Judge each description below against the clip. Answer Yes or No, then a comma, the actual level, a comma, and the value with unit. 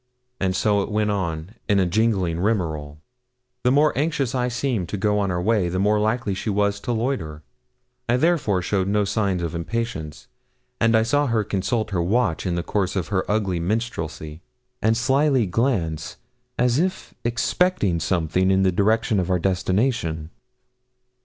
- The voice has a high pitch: No, low, 100 Hz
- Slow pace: No, average, 170 wpm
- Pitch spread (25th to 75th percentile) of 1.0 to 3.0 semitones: No, average, 4.5 semitones